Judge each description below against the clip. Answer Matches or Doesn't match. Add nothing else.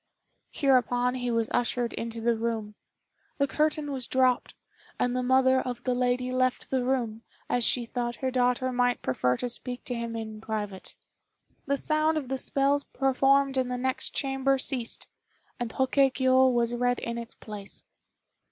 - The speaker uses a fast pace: Doesn't match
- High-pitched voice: Matches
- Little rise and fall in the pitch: Matches